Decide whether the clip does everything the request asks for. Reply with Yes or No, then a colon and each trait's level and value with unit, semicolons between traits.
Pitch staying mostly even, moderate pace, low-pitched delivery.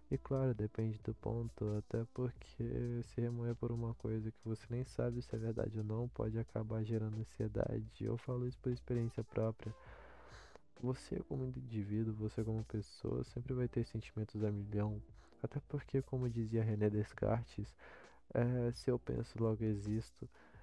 Yes: narrow, 2.0 semitones; average, 160 wpm; low, 115 Hz